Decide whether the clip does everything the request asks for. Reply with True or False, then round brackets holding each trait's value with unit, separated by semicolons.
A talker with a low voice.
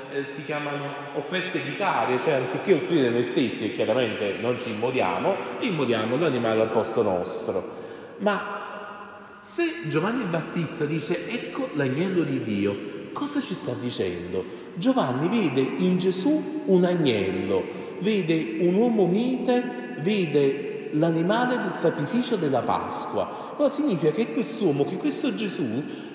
False (175 Hz)